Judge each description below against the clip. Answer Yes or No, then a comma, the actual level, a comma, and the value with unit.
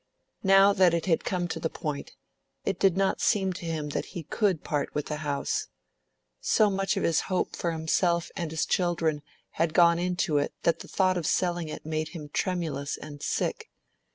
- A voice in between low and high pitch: Yes, medium, 170 Hz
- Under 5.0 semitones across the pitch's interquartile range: Yes, average, 2.9 semitones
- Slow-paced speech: No, average, 195 wpm